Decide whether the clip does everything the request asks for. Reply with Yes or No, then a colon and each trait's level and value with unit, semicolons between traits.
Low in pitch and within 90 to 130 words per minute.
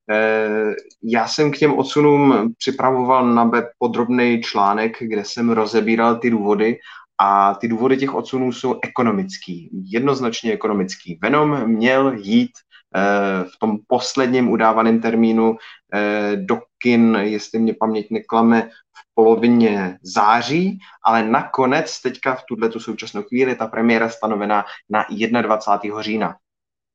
Yes: low, 115 Hz; average, 120 wpm